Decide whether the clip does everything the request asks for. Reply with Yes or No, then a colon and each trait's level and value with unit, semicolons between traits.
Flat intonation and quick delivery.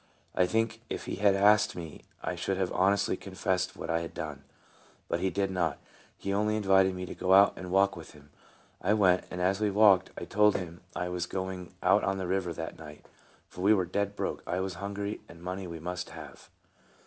Yes: narrow, 1.9 semitones; fast, 220 wpm